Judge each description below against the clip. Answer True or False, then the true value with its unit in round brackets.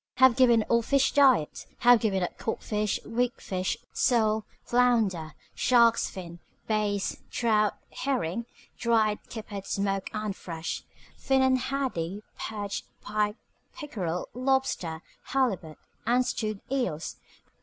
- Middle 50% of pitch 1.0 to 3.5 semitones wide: False (4.1 semitones)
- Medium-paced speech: False (115 wpm)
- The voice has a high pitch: True (215 Hz)